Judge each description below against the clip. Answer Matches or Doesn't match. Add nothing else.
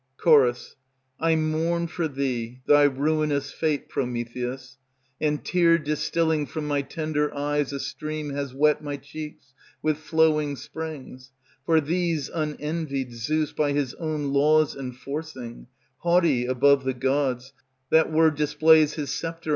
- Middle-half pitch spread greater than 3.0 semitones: Doesn't match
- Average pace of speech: Doesn't match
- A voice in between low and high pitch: Matches